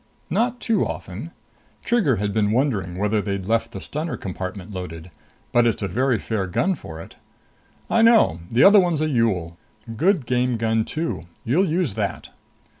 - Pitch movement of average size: No, wide, 8.1 semitones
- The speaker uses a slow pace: No, average, 170 wpm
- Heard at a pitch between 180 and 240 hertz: No, low, 115 Hz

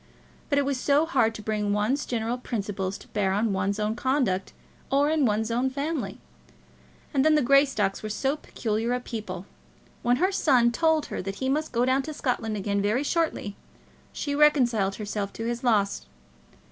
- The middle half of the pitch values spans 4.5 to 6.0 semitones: Yes, average, 5.0 semitones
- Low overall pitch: No, high, 235 Hz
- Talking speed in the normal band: Yes, average, 185 wpm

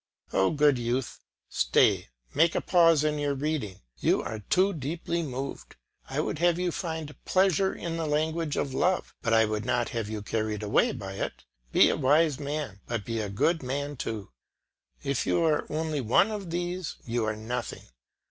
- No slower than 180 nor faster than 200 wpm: Yes, average, 185 wpm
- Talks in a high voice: No, medium, 145 Hz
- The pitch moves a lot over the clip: Yes, wide, 6.2 semitones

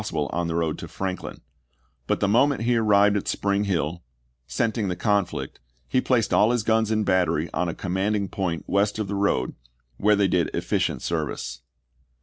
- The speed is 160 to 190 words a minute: Yes, average, 180 wpm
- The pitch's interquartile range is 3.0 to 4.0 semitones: Yes, average, 3.5 semitones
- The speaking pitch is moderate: No, low, 100 Hz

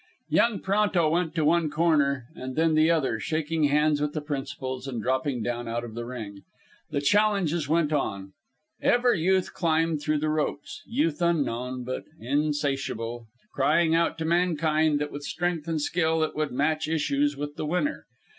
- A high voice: No, medium, 150 Hz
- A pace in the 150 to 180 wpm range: Yes, average, 170 wpm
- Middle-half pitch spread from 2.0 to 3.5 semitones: Yes, average, 3.2 semitones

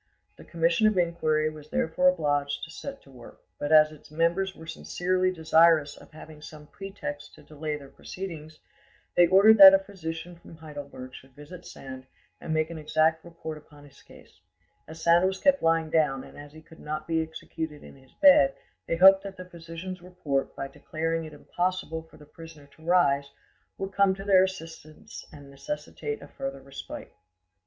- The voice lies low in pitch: No, medium, 160 Hz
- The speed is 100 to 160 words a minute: No, average, 185 wpm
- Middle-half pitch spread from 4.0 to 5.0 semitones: No, average, 3.3 semitones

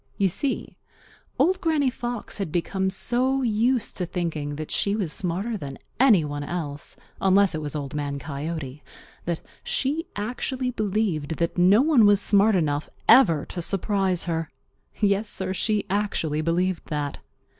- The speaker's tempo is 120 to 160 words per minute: Yes, average, 155 wpm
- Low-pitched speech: No, high, 190 Hz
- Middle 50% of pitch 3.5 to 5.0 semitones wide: No, wide, 5.6 semitones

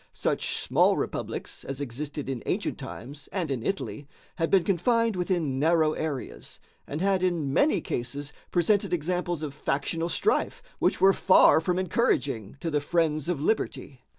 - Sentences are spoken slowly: No, average, 155 wpm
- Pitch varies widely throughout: No, average, 4.2 semitones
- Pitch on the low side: No, medium, 160 Hz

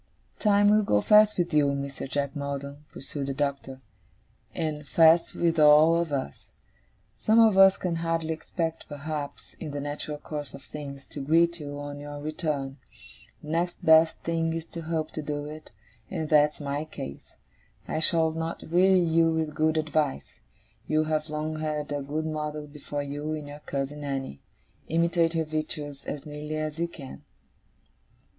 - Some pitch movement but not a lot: No, narrow, 2.1 semitones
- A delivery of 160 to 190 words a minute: Yes, average, 170 wpm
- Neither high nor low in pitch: Yes, medium, 155 Hz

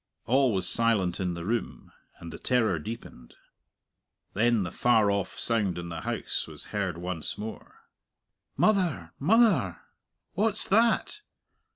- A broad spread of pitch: Yes, wide, 6.6 semitones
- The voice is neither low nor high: No, low, 110 Hz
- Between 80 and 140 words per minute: Yes, slow, 135 wpm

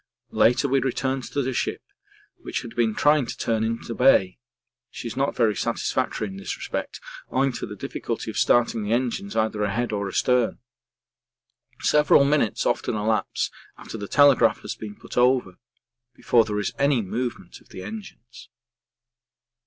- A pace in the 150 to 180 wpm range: Yes, average, 165 wpm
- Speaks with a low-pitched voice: Yes, low, 120 Hz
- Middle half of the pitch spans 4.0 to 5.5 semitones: No, average, 3.6 semitones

